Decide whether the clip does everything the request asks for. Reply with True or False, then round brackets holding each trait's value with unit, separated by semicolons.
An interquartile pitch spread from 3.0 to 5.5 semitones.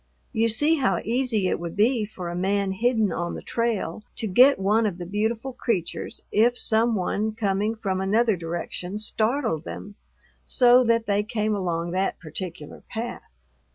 True (3.7 semitones)